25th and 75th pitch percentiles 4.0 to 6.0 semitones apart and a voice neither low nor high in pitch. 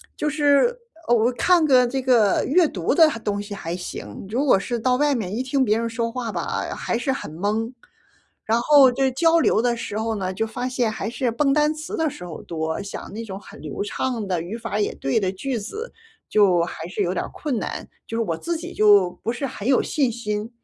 No: average, 4.7 semitones; high, 230 Hz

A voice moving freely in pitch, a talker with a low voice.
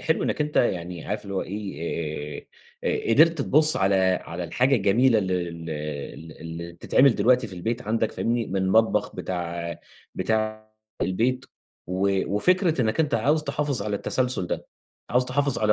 Yes: wide, 6.4 semitones; low, 105 Hz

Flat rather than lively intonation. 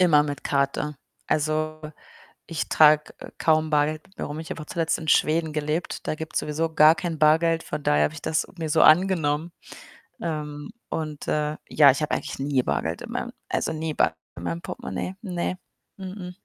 Yes: narrow, 1.7 semitones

